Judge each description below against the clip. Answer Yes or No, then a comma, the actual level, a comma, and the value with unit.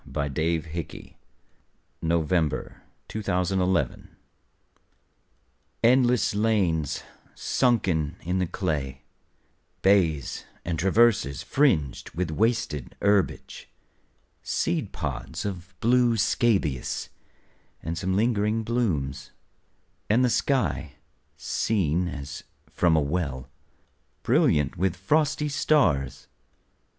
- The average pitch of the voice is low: Yes, very low, 90 Hz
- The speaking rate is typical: No, slow, 85 wpm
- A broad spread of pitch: Yes, wide, 6.4 semitones